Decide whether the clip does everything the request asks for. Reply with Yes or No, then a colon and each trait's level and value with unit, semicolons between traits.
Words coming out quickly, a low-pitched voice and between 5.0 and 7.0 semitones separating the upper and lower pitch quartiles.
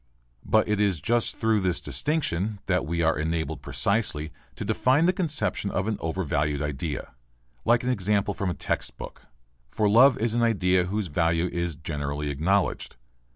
No: average, 165 wpm; very low, 95 Hz; average, 5.3 semitones